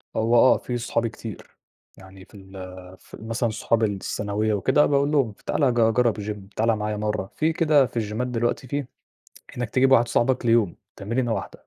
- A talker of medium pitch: No, low, 115 Hz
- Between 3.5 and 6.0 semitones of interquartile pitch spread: No, average, 3.1 semitones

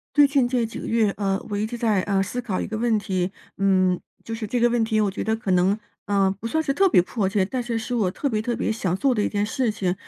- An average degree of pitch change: Yes, average, 3.6 semitones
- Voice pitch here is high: Yes, high, 215 Hz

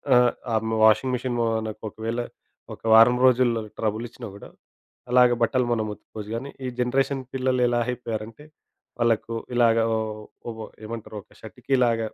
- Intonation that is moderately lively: No, narrow, 2.0 semitones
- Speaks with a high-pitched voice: No, low, 120 Hz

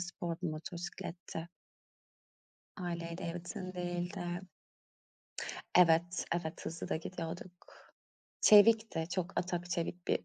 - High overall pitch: No, medium, 175 Hz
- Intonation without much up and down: Yes, narrow, 1.3 semitones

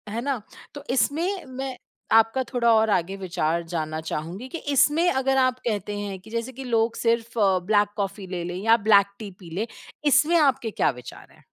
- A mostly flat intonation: No, average, 5.2 semitones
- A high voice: Yes, high, 225 Hz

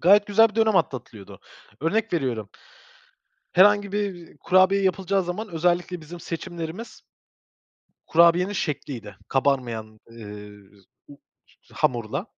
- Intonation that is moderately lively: No, wide, 7.9 semitones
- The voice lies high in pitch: No, medium, 170 Hz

